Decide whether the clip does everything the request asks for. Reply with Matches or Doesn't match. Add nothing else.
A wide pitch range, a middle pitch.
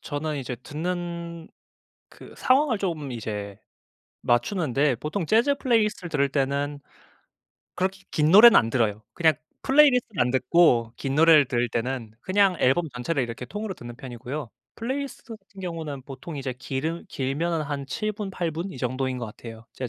Matches